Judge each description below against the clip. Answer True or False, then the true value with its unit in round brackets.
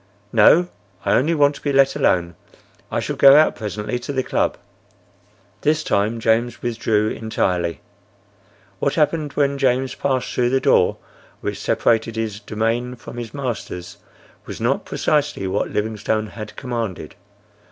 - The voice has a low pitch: True (120 Hz)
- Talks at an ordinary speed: True (145 wpm)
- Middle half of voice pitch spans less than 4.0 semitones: False (4.3 semitones)